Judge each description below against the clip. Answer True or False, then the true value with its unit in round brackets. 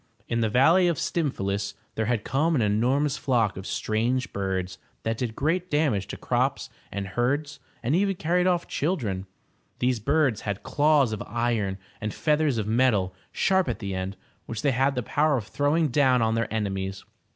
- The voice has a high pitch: False (120 Hz)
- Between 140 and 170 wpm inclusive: False (185 wpm)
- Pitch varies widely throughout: True (6.0 semitones)